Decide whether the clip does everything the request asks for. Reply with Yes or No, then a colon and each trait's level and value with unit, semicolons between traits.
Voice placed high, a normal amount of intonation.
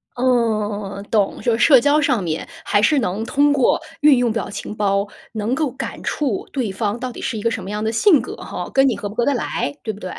Yes: high, 230 Hz; average, 4.2 semitones